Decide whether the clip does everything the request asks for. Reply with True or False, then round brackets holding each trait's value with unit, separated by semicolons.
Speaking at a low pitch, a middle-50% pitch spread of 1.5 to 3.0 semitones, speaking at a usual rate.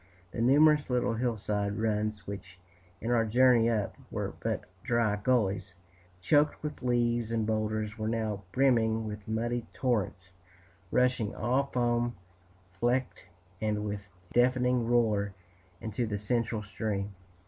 False (115 Hz; 2.5 semitones; 125 wpm)